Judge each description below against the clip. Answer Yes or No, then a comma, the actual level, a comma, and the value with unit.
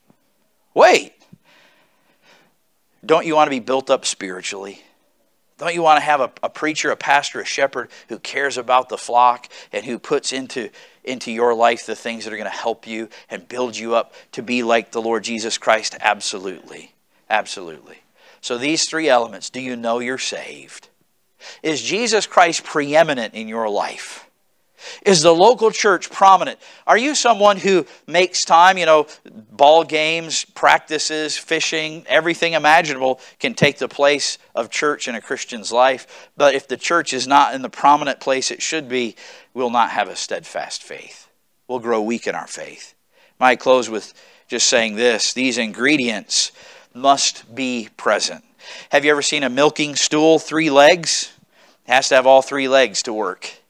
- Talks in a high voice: No, low, 135 Hz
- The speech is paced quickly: No, average, 170 wpm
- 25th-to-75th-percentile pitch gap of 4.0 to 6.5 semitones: Yes, average, 4.5 semitones